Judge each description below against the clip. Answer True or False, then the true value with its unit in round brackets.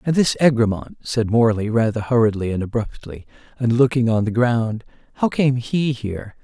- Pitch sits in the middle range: False (120 Hz)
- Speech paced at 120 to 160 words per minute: False (170 wpm)